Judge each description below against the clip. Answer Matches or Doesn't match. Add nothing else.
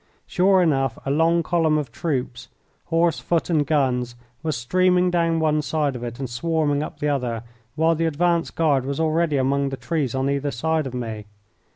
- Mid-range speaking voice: Matches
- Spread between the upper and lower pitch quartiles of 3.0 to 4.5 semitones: Matches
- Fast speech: Doesn't match